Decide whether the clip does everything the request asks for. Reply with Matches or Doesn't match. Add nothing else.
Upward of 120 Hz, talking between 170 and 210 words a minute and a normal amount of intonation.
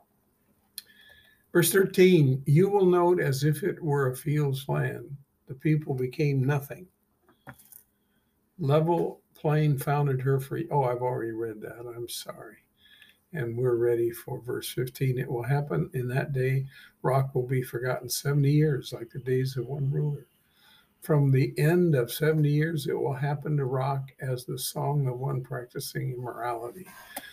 Doesn't match